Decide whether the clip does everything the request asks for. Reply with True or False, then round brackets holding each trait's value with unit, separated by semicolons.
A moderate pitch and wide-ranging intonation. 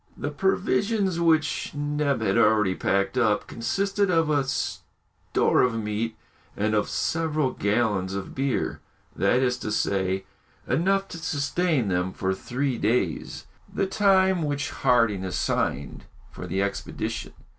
False (130 Hz; 7.6 semitones)